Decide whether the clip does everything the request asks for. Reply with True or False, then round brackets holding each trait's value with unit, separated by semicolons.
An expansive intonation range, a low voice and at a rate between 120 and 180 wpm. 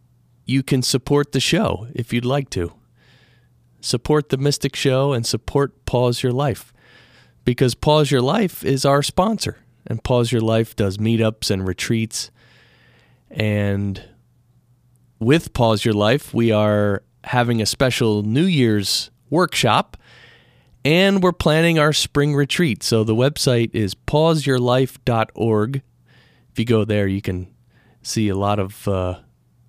False (4.0 semitones; 120 Hz; 135 wpm)